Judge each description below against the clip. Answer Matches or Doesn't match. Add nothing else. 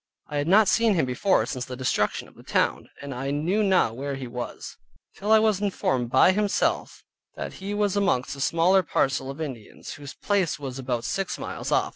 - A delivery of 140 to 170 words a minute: Doesn't match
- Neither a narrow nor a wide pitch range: Doesn't match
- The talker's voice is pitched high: Doesn't match